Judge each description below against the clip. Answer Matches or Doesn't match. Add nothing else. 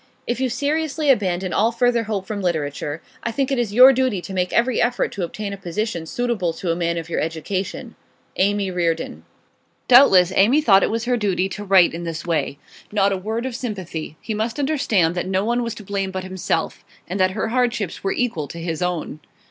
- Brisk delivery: Matches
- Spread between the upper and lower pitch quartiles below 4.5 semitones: Doesn't match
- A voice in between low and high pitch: Doesn't match